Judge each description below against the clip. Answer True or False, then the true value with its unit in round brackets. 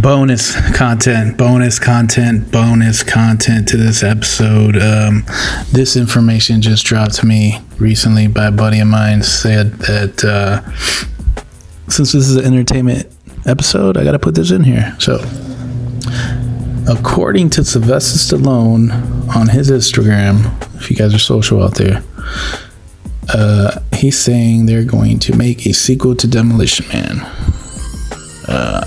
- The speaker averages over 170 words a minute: False (135 wpm)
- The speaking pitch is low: True (115 Hz)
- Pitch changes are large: False (2.6 semitones)